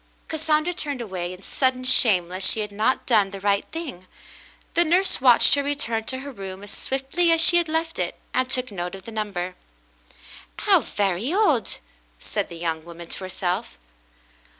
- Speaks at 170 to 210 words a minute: Yes, average, 185 wpm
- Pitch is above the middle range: Yes, high, 225 Hz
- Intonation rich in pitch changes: Yes, wide, 7.4 semitones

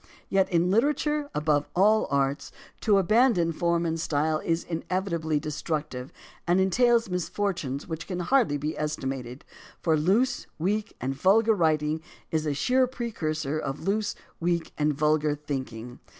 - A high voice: No, medium, 165 Hz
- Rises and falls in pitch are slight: No, average, 4.8 semitones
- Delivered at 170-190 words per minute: No, average, 140 wpm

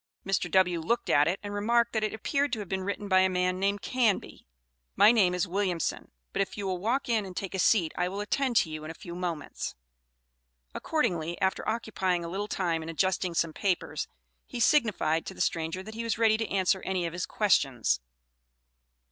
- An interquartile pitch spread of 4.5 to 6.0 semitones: No, average, 3.8 semitones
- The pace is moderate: No, fast, 210 wpm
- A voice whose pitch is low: No, high, 190 Hz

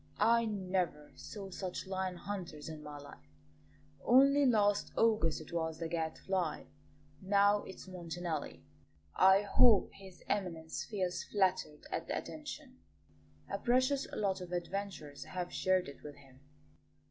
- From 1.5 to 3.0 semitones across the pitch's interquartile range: No, average, 4.0 semitones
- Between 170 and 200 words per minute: No, slow, 135 wpm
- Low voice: No, medium, 185 Hz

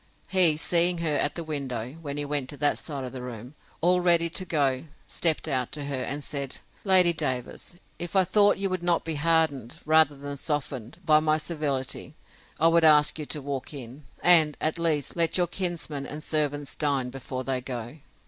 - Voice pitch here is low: No, medium, 150 Hz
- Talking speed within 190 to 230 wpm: Yes, average, 195 wpm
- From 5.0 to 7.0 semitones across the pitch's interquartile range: No, average, 3.5 semitones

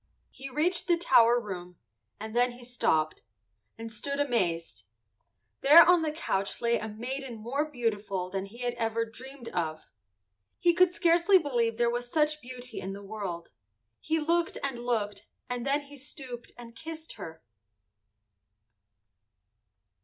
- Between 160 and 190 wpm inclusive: No, average, 145 wpm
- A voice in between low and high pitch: No, high, 245 Hz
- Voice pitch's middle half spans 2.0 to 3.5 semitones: No, average, 5.1 semitones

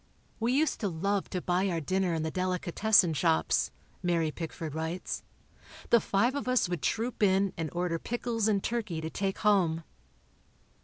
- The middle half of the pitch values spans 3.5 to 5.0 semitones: Yes, average, 4.2 semitones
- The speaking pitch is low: No, medium, 185 Hz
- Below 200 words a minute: Yes, average, 165 wpm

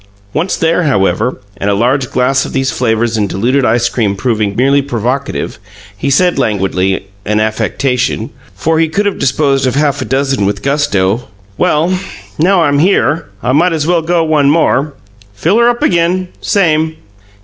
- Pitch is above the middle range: No, low, 135 Hz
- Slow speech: No, average, 170 wpm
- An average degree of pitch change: No, wide, 5.9 semitones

